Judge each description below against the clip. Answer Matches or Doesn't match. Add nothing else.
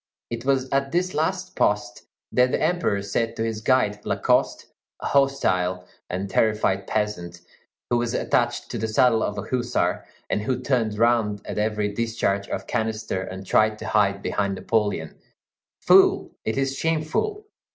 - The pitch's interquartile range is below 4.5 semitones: Matches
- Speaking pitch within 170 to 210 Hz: Doesn't match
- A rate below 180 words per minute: Matches